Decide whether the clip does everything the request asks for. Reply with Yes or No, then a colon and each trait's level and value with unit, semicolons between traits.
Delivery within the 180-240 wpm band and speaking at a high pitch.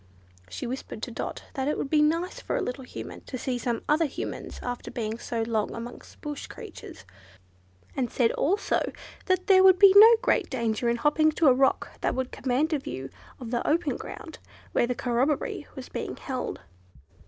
Yes: average, 190 wpm; very high, 265 Hz